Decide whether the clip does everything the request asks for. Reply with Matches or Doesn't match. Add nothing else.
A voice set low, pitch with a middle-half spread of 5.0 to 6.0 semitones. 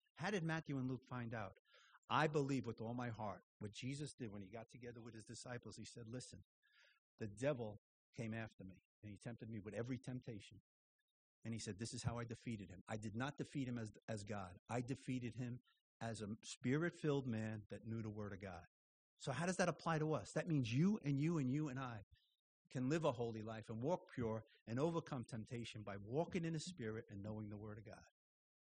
Doesn't match